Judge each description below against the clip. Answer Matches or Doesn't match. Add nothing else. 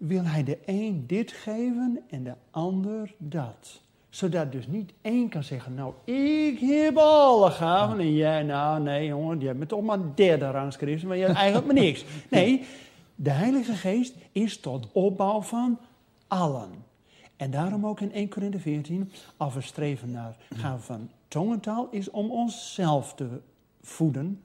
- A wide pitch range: Matches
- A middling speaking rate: Matches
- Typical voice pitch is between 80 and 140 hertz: Doesn't match